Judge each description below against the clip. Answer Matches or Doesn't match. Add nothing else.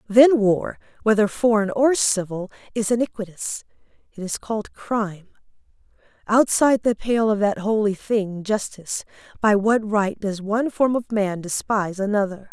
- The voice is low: Doesn't match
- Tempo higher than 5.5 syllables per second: Doesn't match